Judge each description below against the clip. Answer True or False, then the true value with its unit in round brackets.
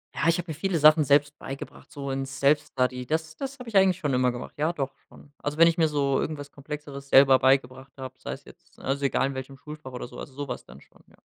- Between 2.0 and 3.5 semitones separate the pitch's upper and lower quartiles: True (2.6 semitones)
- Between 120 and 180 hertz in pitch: True (140 Hz)